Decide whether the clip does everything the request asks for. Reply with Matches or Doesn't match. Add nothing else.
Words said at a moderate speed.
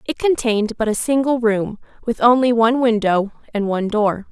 Matches